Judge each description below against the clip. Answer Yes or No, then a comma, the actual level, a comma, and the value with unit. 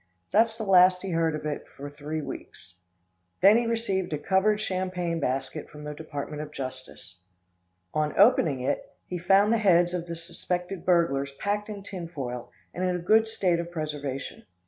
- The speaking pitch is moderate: Yes, medium, 170 Hz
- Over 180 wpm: No, average, 175 wpm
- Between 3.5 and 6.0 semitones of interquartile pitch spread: Yes, average, 4.4 semitones